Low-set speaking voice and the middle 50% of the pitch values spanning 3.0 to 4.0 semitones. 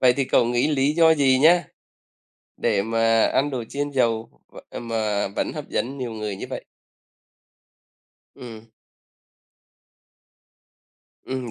Yes: low, 125 Hz; average, 3.6 semitones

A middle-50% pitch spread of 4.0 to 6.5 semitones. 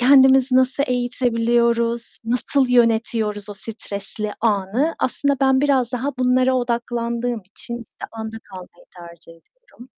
No: narrow, 2.5 semitones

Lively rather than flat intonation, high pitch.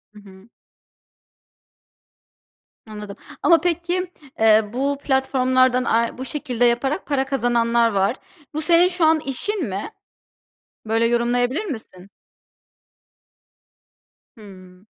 No: average, 4.8 semitones; high, 245 Hz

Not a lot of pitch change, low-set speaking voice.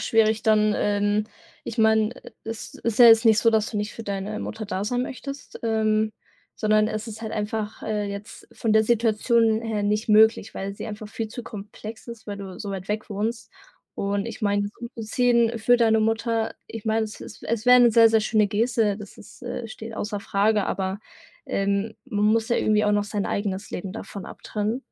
No: narrow, 1.5 semitones; high, 215 Hz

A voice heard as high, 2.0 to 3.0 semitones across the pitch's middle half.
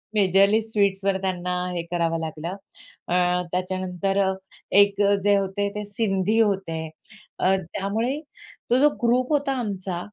Yes: high, 195 Hz; narrow, 2.5 semitones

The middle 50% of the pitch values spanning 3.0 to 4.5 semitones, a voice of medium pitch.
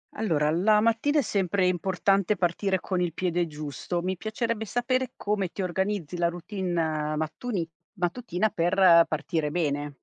Yes: average, 3.8 semitones; medium, 180 Hz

